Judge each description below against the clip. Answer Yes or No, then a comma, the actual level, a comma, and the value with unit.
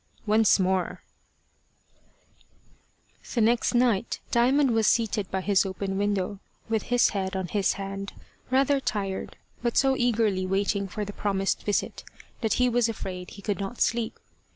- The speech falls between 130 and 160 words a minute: Yes, average, 150 wpm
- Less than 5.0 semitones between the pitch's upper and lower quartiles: Yes, average, 3.4 semitones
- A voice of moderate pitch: No, high, 205 Hz